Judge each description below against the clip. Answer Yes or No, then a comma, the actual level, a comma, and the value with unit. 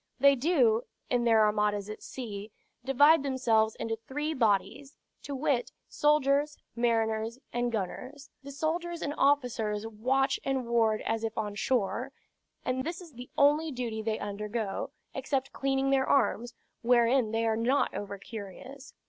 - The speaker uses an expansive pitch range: No, average, 3.8 semitones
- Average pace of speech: Yes, average, 150 wpm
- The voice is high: Yes, high, 245 Hz